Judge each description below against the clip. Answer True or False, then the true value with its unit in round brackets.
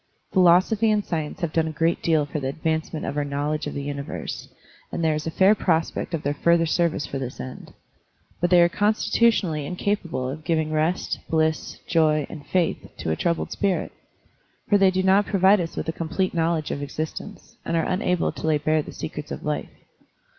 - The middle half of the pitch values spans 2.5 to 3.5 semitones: True (3.0 semitones)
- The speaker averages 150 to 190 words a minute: False (205 wpm)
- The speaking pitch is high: False (165 Hz)